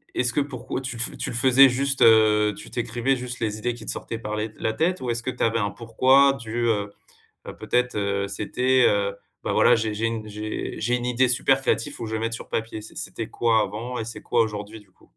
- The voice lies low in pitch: Yes, low, 115 Hz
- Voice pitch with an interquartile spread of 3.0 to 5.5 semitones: No, narrow, 2.5 semitones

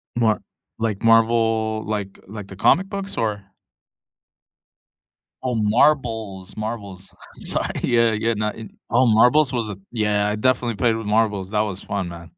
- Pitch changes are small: Yes, narrow, 2.2 semitones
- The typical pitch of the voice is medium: No, low, 110 Hz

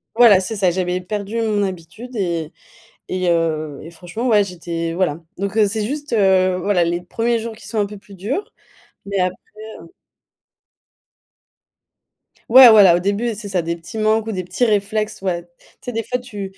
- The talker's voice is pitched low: No, high, 200 Hz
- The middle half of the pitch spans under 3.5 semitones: No, average, 3.8 semitones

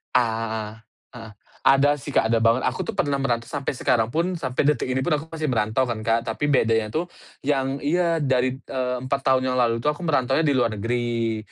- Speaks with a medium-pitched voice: No, low, 130 Hz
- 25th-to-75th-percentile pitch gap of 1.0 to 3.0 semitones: No, average, 3.8 semitones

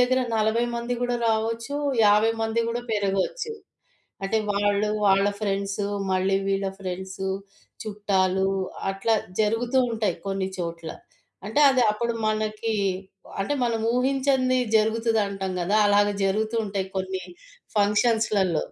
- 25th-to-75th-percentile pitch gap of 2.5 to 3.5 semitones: Yes, average, 2.8 semitones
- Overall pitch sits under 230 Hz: Yes, high, 210 Hz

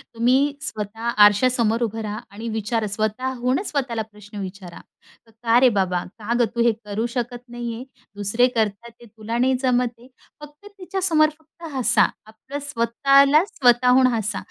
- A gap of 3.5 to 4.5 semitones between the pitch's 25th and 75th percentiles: No, average, 3.1 semitones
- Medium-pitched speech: No, high, 235 Hz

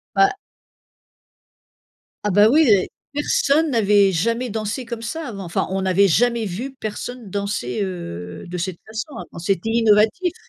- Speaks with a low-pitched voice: No, high, 215 Hz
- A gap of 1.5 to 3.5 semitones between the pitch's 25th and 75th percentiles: No, average, 4.2 semitones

